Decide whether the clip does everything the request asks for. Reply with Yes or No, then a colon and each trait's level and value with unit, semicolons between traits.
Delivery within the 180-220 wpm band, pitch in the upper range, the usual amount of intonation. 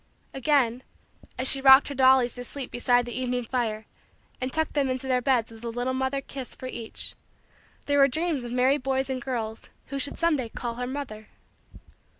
No: average, 195 wpm; very high, 255 Hz; narrow, 2.0 semitones